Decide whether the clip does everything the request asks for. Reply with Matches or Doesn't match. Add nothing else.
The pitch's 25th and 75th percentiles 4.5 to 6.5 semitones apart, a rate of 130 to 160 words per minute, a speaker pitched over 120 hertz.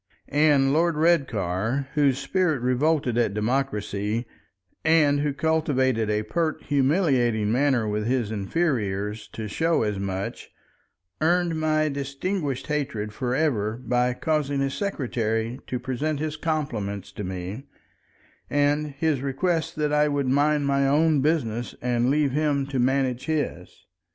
Matches